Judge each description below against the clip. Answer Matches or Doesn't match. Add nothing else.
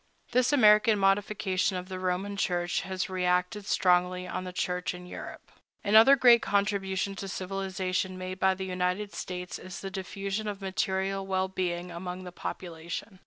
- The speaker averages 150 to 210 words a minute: Matches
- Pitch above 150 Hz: Matches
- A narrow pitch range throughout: Matches